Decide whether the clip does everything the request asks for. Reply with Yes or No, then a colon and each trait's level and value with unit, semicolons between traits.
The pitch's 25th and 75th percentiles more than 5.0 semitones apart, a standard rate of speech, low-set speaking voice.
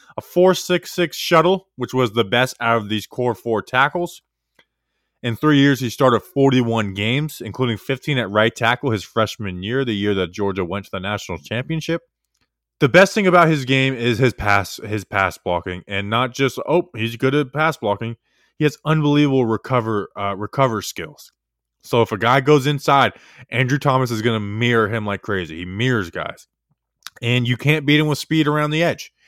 Yes: wide, 5.4 semitones; average, 195 wpm; low, 125 Hz